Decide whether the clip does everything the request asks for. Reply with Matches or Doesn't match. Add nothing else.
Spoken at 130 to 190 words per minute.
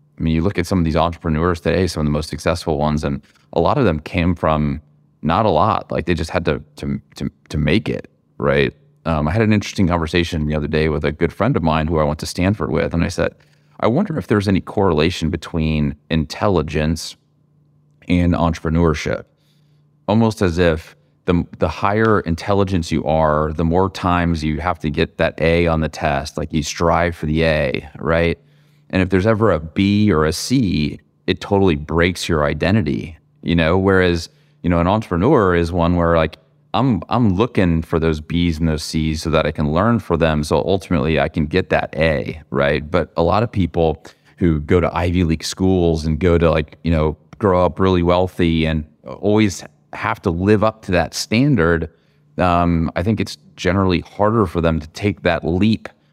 Doesn't match